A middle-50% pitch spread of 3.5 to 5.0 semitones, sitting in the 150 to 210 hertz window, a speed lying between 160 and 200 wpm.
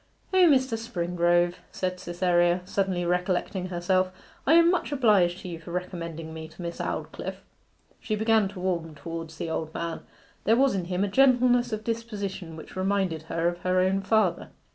Yes: average, 3.8 semitones; medium, 185 Hz; average, 175 wpm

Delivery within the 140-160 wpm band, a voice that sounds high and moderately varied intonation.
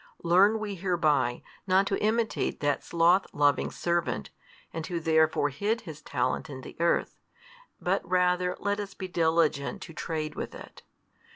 No: average, 155 wpm; medium, 170 Hz; average, 3.6 semitones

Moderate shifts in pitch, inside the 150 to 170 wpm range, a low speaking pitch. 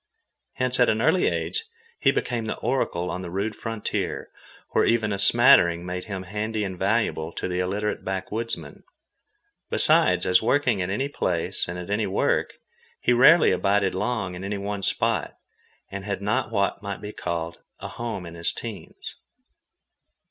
Yes: average, 3.6 semitones; average, 165 wpm; low, 100 Hz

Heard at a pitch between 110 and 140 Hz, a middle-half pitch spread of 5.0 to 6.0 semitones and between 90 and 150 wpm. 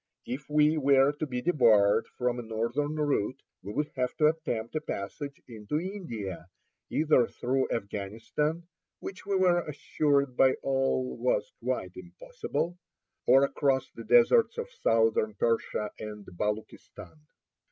Yes: low, 135 Hz; wide, 5.4 semitones; slow, 135 wpm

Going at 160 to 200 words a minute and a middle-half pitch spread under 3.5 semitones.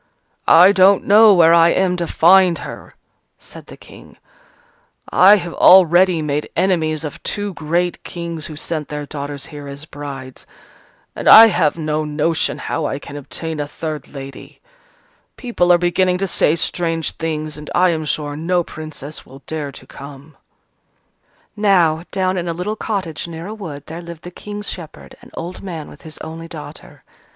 Yes: average, 170 wpm; average, 3.1 semitones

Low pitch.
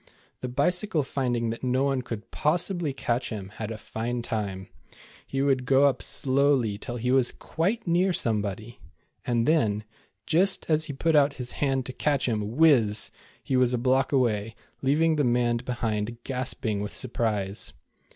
Yes: low, 125 Hz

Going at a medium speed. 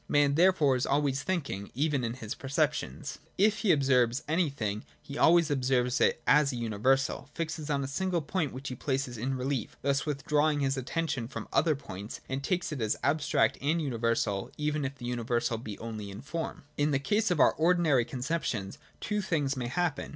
Yes: average, 190 wpm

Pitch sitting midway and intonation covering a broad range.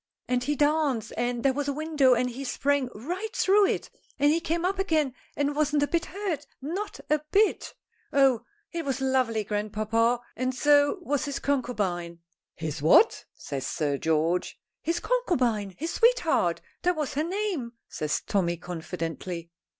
No: very high, 275 Hz; wide, 6.7 semitones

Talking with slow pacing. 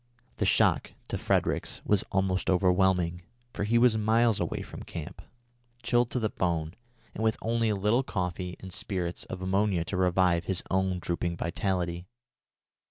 No: average, 165 wpm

